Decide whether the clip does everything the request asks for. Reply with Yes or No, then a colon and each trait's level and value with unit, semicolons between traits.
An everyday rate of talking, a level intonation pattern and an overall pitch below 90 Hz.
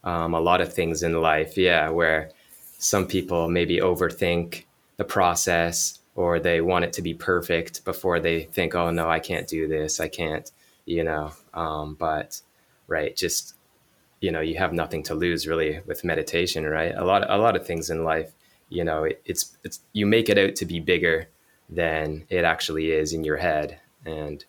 Yes: average, 190 wpm; narrow, 1.4 semitones; very low, 80 Hz